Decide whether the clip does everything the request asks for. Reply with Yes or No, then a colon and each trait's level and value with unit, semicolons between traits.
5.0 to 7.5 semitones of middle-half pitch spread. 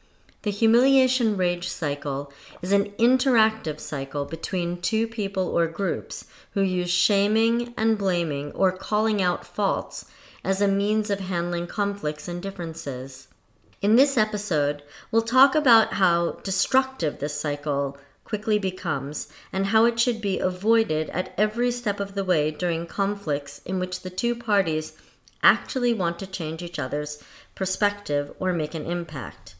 Yes: wide, 5.4 semitones